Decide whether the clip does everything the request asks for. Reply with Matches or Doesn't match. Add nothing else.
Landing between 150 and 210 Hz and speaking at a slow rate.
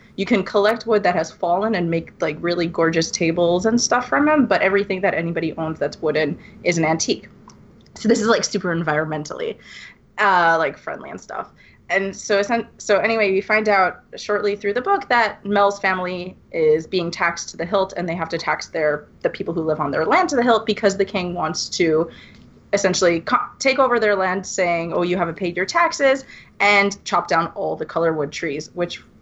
Doesn't match